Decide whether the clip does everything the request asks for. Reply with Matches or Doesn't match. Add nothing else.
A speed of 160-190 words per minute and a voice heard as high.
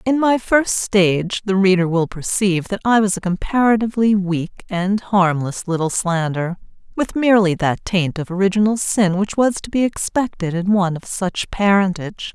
Matches